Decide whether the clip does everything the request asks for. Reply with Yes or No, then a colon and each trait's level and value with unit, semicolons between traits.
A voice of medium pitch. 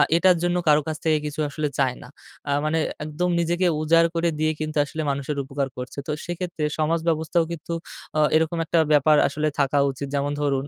Yes: medium, 155 Hz